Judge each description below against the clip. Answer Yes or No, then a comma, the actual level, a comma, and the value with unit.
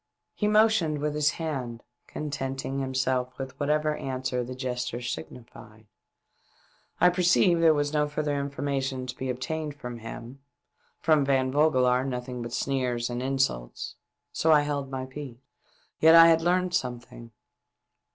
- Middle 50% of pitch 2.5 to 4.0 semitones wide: Yes, average, 3.2 semitones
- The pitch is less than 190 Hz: Yes, low, 135 Hz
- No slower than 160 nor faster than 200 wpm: No, average, 150 wpm